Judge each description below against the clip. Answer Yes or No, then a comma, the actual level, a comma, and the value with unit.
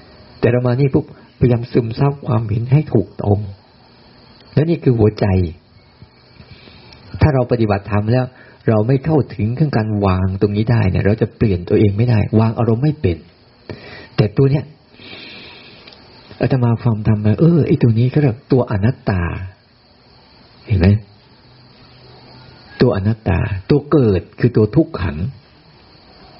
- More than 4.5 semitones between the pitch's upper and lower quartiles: No, average, 3.3 semitones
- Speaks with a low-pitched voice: Yes, low, 120 Hz